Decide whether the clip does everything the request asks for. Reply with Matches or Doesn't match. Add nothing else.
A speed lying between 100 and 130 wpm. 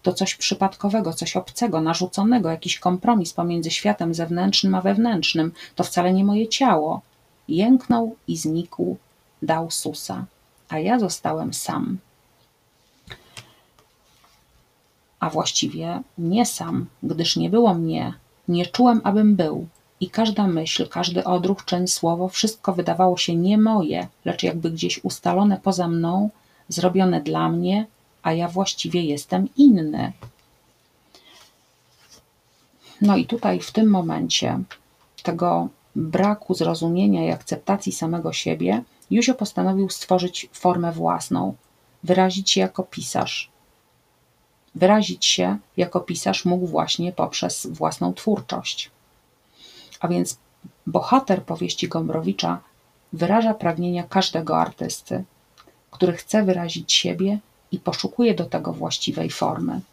Matches